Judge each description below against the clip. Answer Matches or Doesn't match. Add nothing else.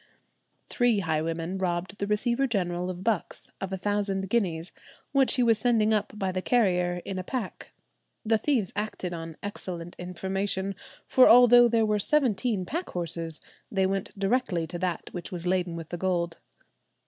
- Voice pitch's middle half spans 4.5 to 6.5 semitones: Doesn't match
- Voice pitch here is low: Doesn't match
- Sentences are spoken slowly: Doesn't match